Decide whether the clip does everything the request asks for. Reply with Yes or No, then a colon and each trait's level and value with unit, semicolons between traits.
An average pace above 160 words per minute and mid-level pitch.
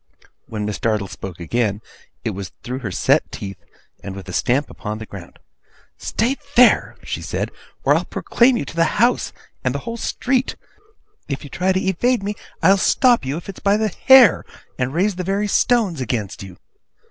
Yes: average, 190 wpm; medium, 165 Hz